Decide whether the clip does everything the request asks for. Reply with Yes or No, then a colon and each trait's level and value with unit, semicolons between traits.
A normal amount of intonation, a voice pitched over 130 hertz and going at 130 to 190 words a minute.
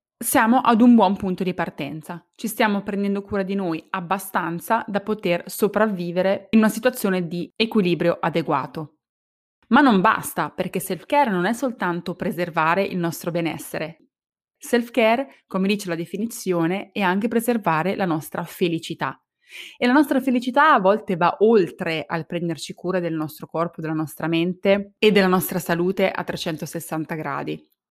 Yes: average, 4.0 semitones; medium, 185 Hz; average, 150 wpm